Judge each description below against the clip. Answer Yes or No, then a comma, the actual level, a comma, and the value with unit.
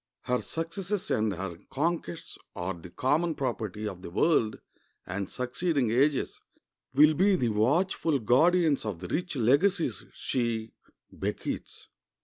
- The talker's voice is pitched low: Yes, low, 130 Hz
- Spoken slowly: Yes, slow, 125 wpm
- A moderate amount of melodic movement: No, wide, 7.4 semitones